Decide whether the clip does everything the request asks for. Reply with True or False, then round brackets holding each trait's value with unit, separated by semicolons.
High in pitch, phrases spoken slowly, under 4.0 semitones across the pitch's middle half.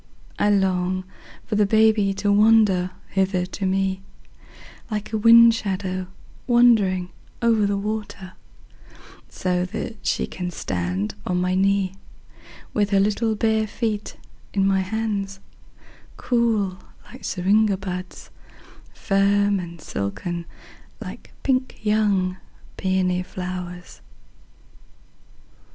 True (195 Hz; 95 wpm; 2.6 semitones)